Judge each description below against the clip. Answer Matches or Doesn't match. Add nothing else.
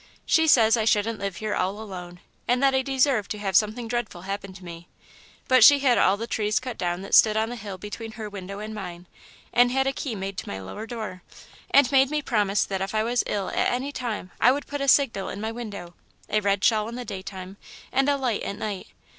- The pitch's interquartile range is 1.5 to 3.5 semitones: Doesn't match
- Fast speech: Matches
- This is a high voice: Matches